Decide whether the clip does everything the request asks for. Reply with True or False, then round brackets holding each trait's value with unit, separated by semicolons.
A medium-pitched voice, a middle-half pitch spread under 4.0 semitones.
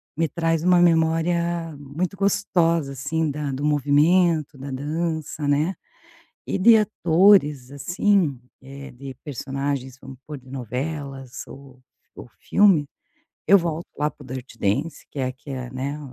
True (150 Hz; 3.6 semitones)